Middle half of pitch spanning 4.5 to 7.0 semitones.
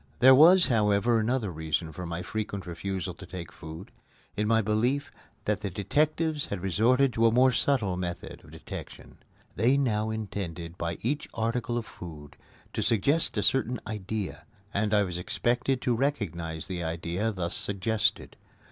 Yes: wide, 5.4 semitones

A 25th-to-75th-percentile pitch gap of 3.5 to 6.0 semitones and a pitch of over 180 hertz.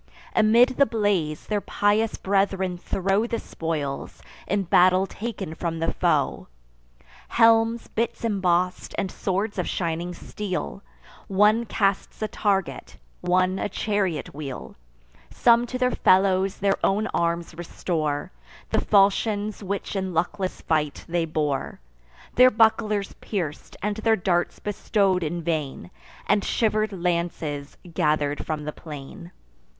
Yes: average, 3.9 semitones; high, 190 Hz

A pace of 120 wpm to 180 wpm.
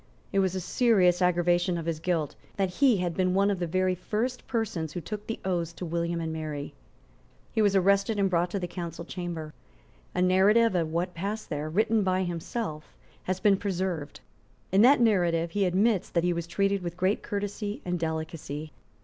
No: average, 190 wpm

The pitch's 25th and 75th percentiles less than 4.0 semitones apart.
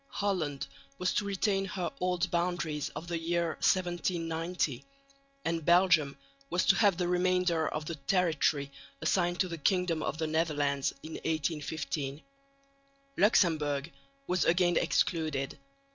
Yes: average, 2.8 semitones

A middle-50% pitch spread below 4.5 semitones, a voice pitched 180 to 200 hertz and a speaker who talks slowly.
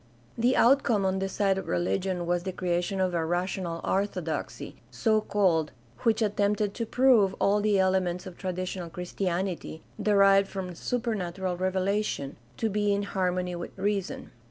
No: narrow, 2.5 semitones; high, 190 Hz; average, 150 wpm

